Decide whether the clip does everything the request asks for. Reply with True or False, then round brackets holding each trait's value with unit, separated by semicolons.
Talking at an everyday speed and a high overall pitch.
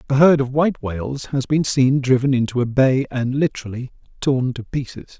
False (195 wpm; 130 Hz)